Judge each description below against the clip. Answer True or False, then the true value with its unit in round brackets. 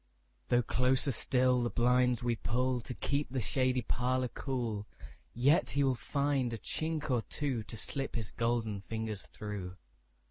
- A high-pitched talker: False (125 Hz)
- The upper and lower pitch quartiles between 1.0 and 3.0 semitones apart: True (2.6 semitones)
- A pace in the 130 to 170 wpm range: True (140 wpm)